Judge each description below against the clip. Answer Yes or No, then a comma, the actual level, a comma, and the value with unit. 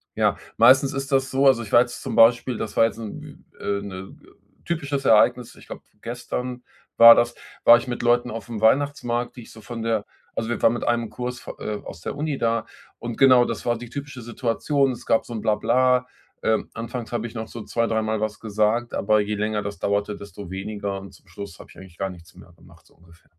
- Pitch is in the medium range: No, low, 115 Hz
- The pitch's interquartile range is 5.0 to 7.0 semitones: No, average, 2.8 semitones